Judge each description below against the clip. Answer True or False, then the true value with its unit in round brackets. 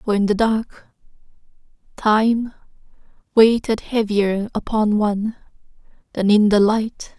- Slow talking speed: True (110 wpm)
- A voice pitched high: True (215 Hz)